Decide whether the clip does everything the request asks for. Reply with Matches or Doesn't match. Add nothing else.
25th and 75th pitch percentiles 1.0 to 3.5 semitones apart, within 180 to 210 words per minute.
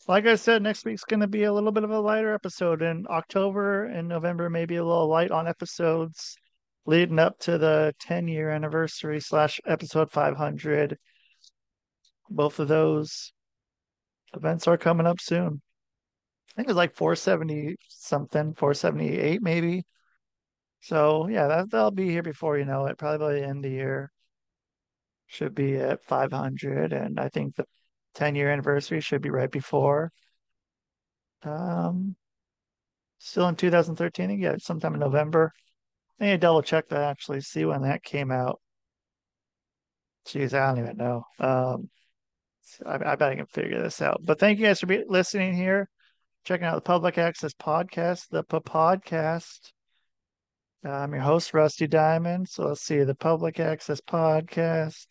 Doesn't match